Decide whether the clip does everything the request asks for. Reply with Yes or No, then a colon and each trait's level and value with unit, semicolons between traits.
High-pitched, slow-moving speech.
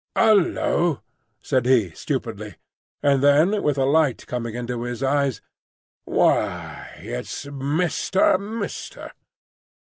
No: medium, 140 Hz; slow, 95 wpm